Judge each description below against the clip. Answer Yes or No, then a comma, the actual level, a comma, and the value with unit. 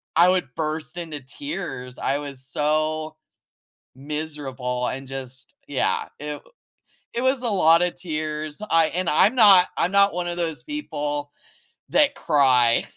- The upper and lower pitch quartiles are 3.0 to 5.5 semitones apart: Yes, average, 3.9 semitones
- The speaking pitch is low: No, medium, 155 Hz